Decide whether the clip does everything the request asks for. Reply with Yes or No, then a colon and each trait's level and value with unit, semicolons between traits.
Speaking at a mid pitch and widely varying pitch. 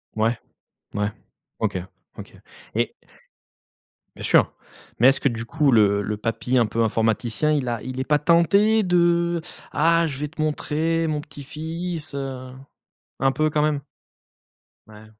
Yes: medium, 145 Hz; wide, 5.8 semitones